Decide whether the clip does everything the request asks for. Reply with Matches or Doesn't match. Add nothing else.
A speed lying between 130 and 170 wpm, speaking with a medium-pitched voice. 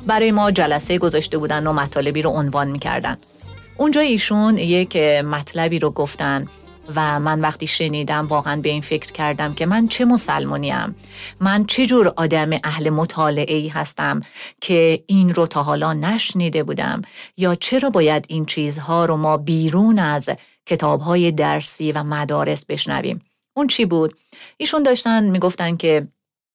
Matches